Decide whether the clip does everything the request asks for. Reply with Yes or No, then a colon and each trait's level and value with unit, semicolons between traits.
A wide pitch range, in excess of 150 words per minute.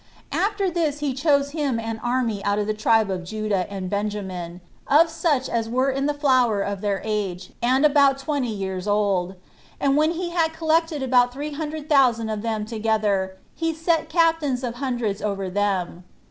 Yes: wide, 6.4 semitones; average, 180 wpm